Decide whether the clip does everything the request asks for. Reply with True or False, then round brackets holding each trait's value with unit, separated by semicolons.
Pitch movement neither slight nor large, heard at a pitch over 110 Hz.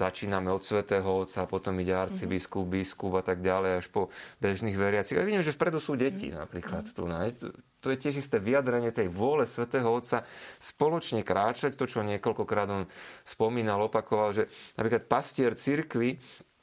False (4.8 semitones; 105 Hz)